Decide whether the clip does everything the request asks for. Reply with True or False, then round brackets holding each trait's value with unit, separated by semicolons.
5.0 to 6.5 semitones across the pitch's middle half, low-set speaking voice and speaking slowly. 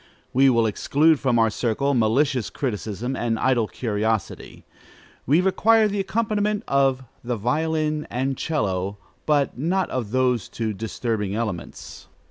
True (5.3 semitones; 130 Hz; 130 wpm)